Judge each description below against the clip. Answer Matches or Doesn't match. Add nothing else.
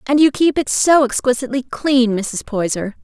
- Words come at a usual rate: Matches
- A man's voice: Doesn't match